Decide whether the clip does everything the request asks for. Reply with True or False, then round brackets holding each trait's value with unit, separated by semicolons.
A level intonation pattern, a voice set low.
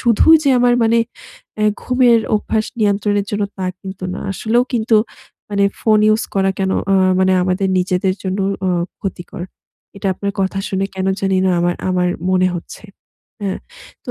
False (2.3 semitones; 195 Hz)